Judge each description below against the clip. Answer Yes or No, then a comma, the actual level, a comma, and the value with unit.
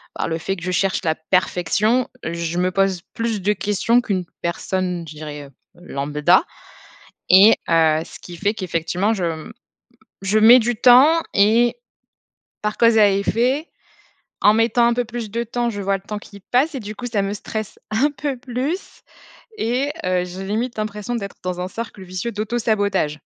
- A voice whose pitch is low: No, high, 205 Hz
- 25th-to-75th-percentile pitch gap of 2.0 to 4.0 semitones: No, average, 4.4 semitones